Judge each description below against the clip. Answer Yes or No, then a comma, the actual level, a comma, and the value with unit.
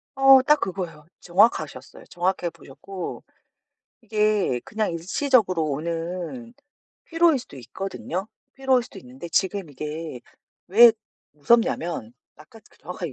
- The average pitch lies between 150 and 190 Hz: Yes, medium, 185 Hz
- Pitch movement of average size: No, wide, 6.1 semitones